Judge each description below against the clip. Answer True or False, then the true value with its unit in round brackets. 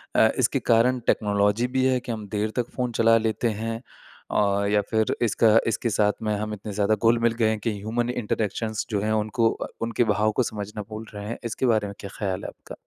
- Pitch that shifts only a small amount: True (2.0 semitones)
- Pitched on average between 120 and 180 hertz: False (110 Hz)